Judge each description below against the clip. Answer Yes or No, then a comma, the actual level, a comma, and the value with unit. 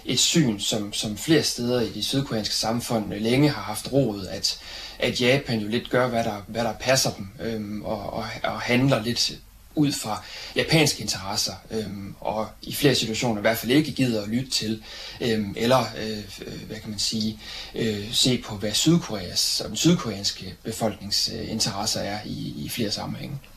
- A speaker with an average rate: Yes, average, 175 wpm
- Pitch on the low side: Yes, low, 110 Hz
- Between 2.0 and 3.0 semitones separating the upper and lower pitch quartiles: Yes, average, 2.7 semitones